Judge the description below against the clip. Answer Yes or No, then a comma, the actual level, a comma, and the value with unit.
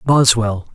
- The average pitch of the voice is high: No, low, 115 Hz